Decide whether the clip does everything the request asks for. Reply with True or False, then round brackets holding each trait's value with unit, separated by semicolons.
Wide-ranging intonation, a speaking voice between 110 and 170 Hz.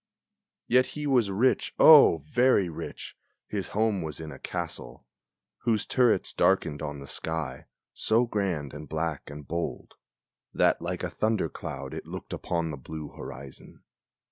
False (6.7 semitones; 85 Hz)